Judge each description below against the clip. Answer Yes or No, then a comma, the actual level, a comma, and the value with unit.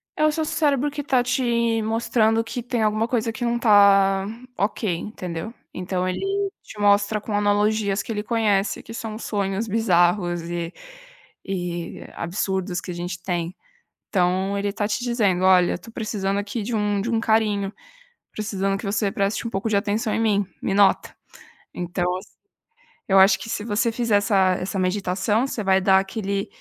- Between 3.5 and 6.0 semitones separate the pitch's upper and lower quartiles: No, average, 2.8 semitones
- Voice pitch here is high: Yes, high, 205 Hz